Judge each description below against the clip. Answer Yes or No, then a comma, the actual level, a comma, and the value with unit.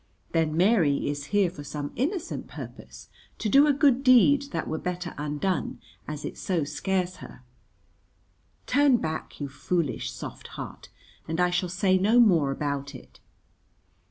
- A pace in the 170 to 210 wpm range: No, average, 155 wpm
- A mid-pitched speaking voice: Yes, medium, 180 Hz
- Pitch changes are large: Yes, wide, 7.3 semitones